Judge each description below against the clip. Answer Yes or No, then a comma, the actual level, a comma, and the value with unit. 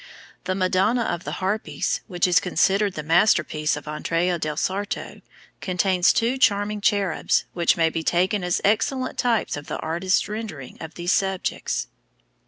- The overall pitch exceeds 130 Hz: Yes, medium, 185 Hz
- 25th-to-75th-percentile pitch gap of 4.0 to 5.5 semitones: No, average, 3.5 semitones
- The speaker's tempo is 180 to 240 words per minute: No, average, 155 wpm